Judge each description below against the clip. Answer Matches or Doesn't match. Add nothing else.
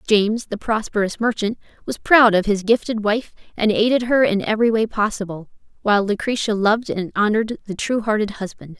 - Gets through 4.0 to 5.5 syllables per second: Doesn't match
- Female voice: Matches